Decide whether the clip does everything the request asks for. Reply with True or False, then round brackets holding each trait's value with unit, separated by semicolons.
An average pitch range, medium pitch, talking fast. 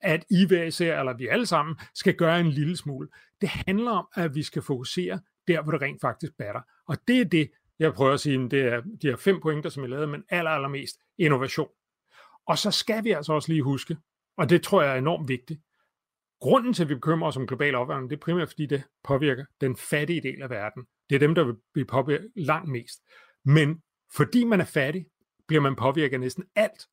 True (4.0 semitones; 155 Hz; 230 wpm)